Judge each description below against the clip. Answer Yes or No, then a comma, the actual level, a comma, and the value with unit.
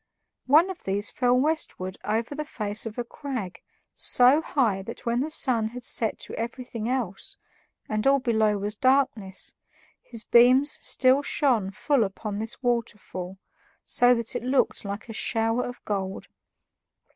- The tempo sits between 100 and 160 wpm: Yes, average, 155 wpm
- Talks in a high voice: Yes, high, 235 Hz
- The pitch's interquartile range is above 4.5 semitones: No, average, 3.6 semitones